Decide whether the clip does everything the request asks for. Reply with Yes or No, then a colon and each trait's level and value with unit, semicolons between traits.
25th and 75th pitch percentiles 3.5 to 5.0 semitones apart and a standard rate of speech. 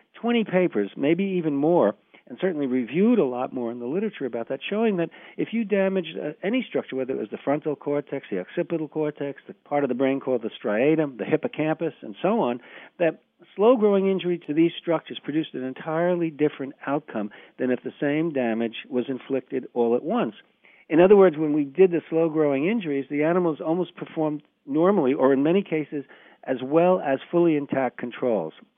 Yes: average, 4.5 semitones; average, 195 wpm